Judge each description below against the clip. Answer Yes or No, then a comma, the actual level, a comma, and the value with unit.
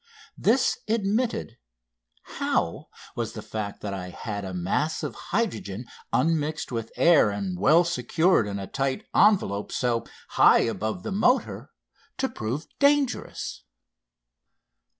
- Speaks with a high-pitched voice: No, low, 125 Hz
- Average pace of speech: No, slow, 125 wpm